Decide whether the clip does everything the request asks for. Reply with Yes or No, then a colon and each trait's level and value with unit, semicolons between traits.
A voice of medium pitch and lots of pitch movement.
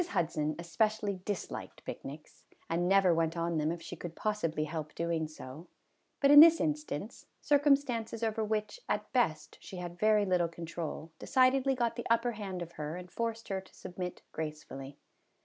Yes: medium, 180 Hz; wide, 5.7 semitones